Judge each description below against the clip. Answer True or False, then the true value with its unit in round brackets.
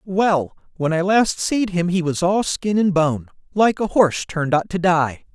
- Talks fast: True (215 wpm)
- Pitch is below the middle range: False (175 Hz)